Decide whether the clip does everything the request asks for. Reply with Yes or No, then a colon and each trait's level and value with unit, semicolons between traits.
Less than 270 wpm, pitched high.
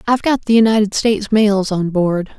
Yes: average, 200 wpm; high, 210 Hz